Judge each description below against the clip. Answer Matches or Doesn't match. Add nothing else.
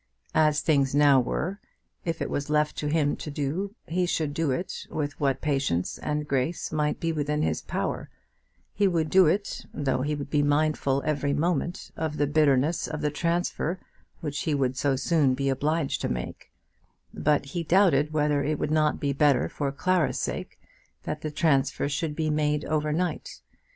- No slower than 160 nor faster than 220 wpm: Matches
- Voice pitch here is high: Doesn't match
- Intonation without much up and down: Matches